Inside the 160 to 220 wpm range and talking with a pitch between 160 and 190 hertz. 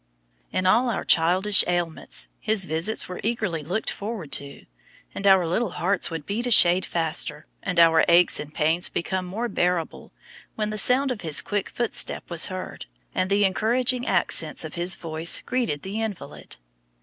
Yes: average, 170 wpm; medium, 185 Hz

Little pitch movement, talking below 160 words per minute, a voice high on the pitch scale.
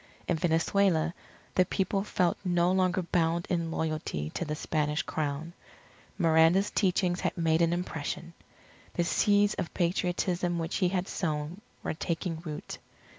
No: narrow, 2.1 semitones; average, 140 wpm; medium, 170 Hz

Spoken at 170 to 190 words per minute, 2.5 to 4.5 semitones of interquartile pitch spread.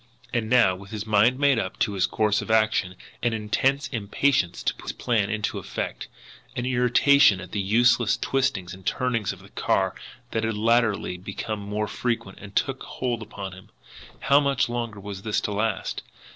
Yes: average, 180 wpm; average, 3.3 semitones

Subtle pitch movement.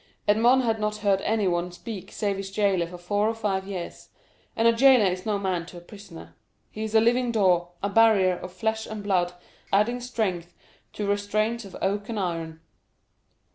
No: average, 3.4 semitones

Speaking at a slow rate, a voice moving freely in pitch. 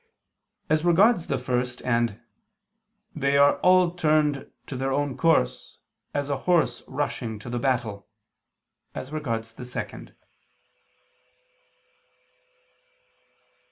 No: slow, 105 wpm; average, 4.2 semitones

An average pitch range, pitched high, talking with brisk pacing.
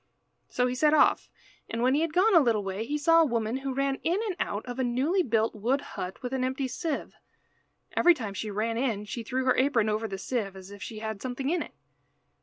Yes: average, 4.3 semitones; very high, 250 Hz; fast, 240 wpm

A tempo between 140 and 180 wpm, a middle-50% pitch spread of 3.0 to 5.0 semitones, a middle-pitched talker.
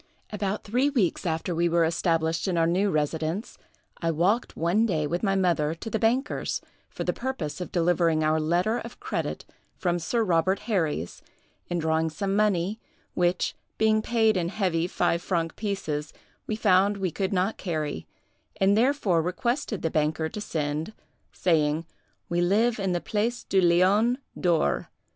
Yes: average, 160 wpm; average, 4.3 semitones; medium, 180 Hz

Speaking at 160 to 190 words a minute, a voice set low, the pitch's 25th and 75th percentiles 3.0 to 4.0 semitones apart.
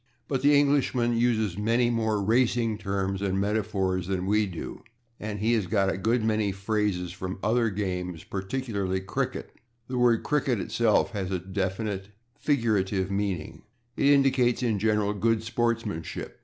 No: average, 150 wpm; low, 105 Hz; average, 3.4 semitones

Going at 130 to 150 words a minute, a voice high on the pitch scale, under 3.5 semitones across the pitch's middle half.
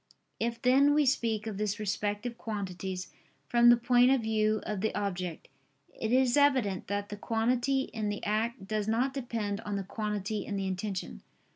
No: average, 175 wpm; high, 215 Hz; average, 2.9 semitones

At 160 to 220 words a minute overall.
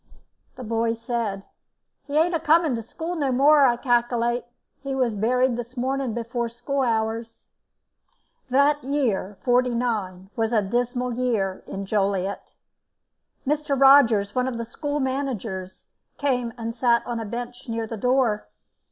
No: average, 145 wpm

